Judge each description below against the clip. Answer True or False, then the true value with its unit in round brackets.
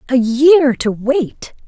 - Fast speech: False (145 wpm)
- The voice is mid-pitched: False (265 Hz)